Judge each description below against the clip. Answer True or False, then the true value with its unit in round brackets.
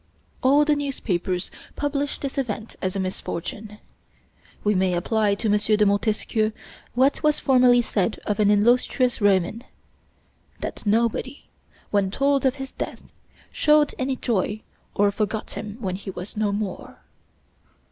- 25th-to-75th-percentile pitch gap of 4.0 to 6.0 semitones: True (4.3 semitones)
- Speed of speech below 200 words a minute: True (140 wpm)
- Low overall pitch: False (215 Hz)